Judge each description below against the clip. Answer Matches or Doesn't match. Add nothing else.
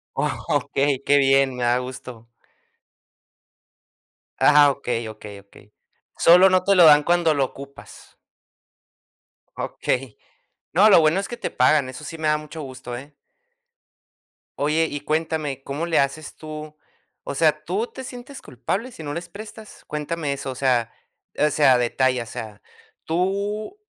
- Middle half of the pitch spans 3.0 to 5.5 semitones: Matches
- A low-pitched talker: Doesn't match